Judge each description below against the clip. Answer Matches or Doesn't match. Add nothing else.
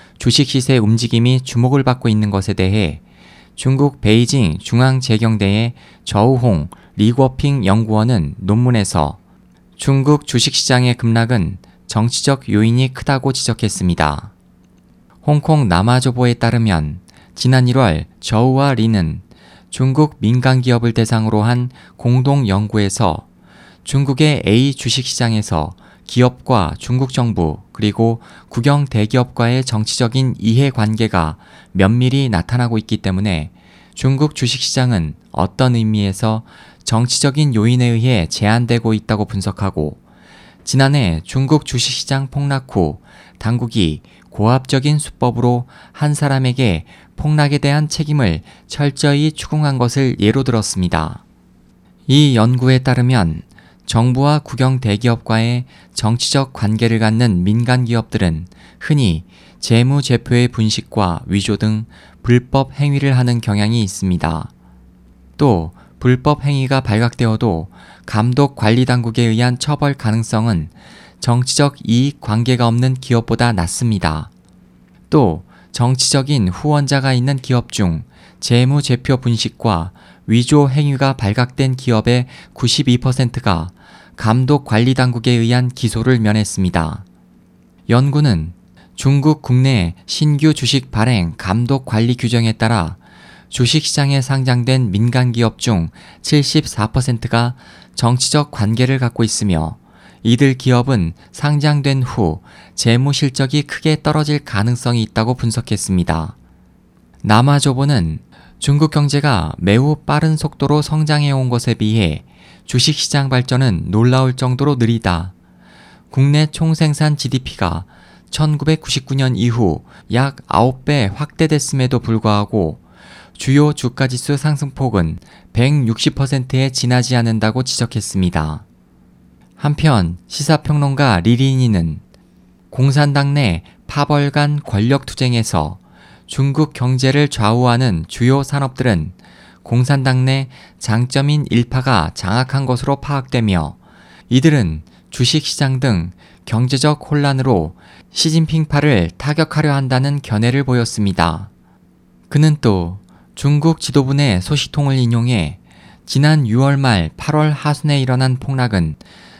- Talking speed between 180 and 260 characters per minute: Matches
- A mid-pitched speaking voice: Doesn't match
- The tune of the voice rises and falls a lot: Doesn't match